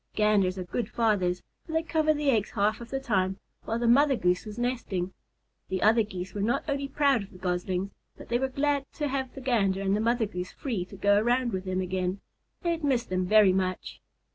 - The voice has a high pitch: Yes, high, 215 Hz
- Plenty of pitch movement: Yes, wide, 5.8 semitones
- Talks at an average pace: No, fast, 225 wpm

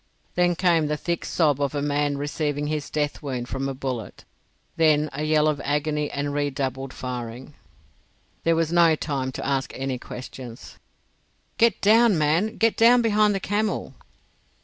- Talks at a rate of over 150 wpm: Yes, average, 160 wpm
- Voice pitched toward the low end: No, medium, 150 Hz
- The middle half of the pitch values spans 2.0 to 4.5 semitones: Yes, average, 3.7 semitones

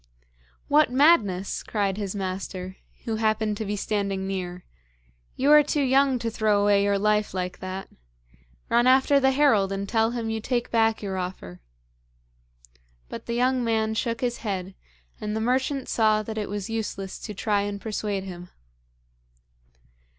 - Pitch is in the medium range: No, high, 215 Hz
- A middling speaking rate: Yes, average, 160 wpm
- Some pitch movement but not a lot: Yes, average, 3.4 semitones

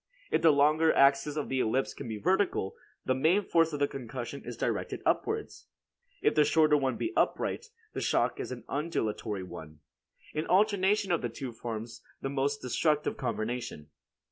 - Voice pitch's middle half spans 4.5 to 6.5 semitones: Yes, average, 5.1 semitones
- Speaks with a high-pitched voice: No, medium, 140 Hz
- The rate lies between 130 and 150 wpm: No, average, 170 wpm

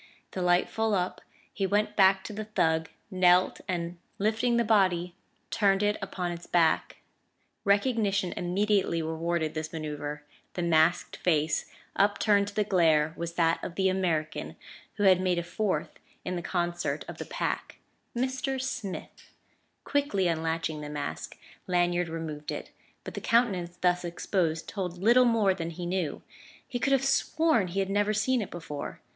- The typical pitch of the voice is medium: Yes, medium, 180 Hz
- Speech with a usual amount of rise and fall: Yes, average, 3.5 semitones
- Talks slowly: No, average, 160 wpm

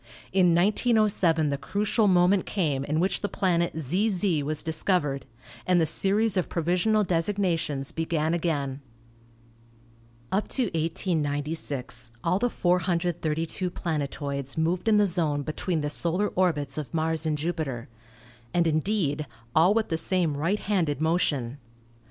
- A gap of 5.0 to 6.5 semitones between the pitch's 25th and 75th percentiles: No, average, 3.7 semitones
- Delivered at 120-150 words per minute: Yes, slow, 135 wpm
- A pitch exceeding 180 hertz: No, medium, 165 Hz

